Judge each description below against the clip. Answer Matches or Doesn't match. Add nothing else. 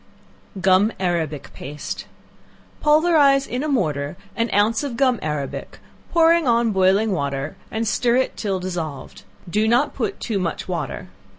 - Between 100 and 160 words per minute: Matches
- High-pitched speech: Matches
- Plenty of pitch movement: Matches